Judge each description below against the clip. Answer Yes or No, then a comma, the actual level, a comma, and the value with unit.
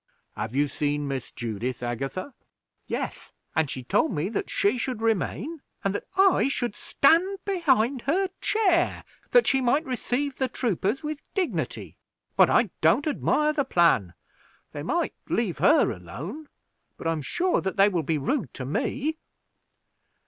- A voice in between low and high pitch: No, high, 235 Hz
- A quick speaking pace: No, average, 155 wpm